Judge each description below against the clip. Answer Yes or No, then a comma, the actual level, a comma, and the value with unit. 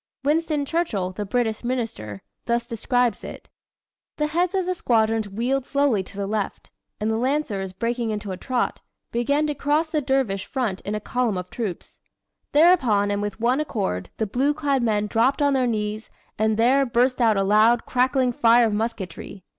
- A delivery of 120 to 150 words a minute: No, average, 180 wpm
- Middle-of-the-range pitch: No, high, 235 Hz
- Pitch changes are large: No, average, 4.5 semitones